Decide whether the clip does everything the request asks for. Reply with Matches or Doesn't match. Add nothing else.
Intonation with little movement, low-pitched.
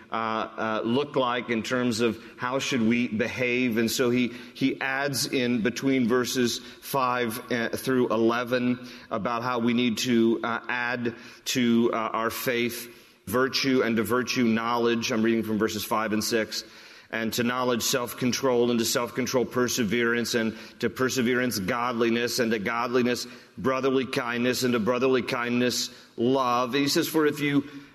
Matches